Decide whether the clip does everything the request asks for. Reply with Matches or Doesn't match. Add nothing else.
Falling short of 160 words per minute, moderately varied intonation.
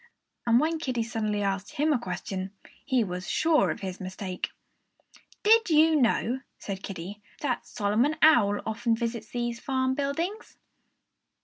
Doesn't match